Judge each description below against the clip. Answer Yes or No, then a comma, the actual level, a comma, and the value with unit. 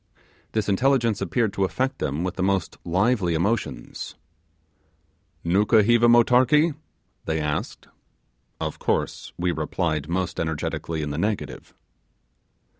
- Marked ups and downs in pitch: Yes, wide, 6.1 semitones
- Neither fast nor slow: No, slow, 115 wpm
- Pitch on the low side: Yes, very low, 95 Hz